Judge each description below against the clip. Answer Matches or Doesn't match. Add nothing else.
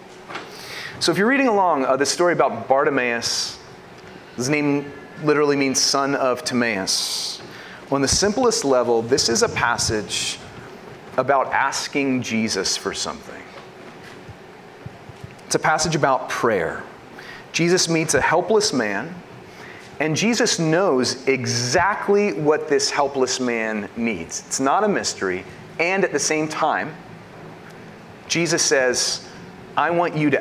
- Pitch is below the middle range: Doesn't match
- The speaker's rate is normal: Doesn't match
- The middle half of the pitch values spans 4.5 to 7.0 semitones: Matches